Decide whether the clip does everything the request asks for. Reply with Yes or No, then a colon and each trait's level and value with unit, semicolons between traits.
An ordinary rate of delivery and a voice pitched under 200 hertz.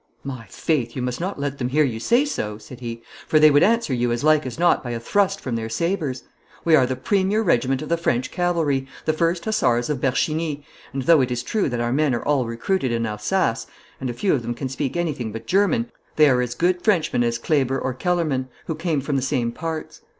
No: fast, 235 wpm; medium, 140 Hz